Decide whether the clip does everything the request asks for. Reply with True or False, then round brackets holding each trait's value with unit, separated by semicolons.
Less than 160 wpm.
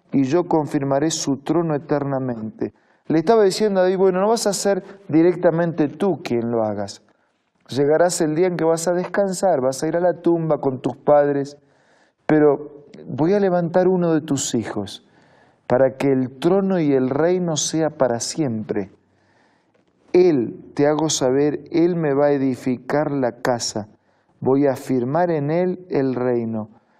False (165 wpm)